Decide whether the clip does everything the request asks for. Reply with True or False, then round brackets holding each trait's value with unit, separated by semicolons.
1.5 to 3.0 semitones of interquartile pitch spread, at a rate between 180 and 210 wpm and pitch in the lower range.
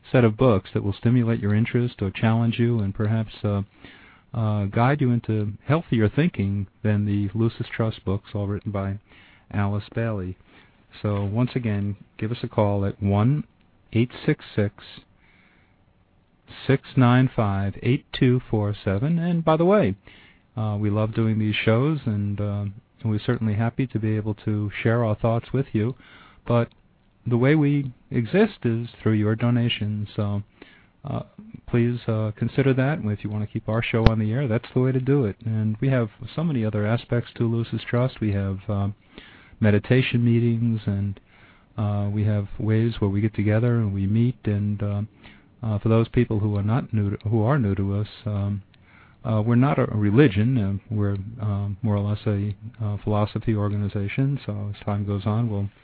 True (2.7 semitones; 185 wpm; 110 Hz)